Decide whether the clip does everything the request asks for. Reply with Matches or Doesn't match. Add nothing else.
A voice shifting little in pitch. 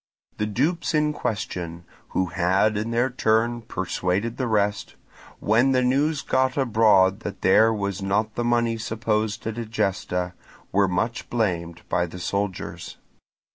Doesn't match